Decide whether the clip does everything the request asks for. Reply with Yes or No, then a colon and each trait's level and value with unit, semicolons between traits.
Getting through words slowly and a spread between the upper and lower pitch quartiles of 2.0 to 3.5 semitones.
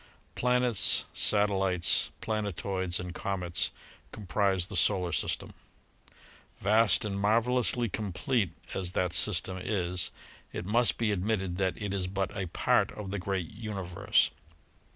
Yes: slow, 125 wpm; average, 2.8 semitones